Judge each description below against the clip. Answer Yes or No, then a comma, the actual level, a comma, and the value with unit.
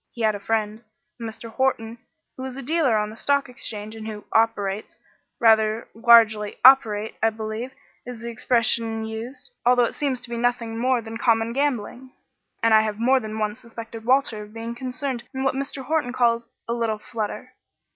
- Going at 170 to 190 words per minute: Yes, average, 185 wpm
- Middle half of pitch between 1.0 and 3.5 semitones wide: Yes, narrow, 2.4 semitones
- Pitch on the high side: Yes, high, 230 Hz